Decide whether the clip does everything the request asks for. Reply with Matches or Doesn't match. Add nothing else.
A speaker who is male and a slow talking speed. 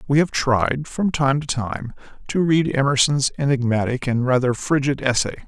Doesn't match